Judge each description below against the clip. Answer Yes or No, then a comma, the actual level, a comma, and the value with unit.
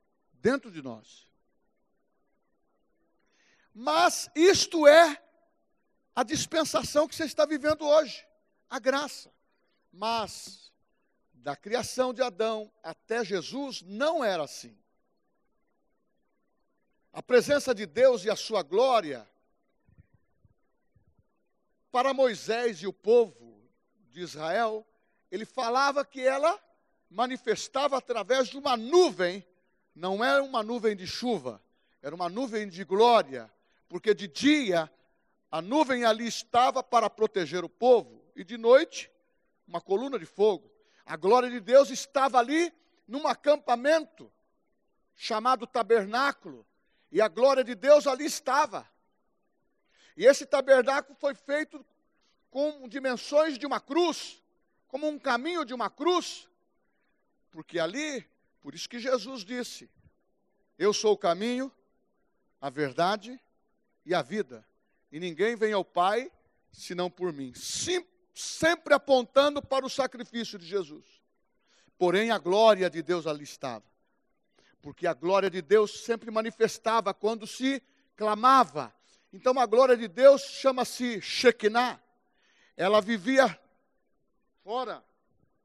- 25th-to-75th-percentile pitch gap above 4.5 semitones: Yes, average, 5.3 semitones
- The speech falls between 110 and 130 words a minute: Yes, slow, 120 wpm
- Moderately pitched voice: No, high, 245 Hz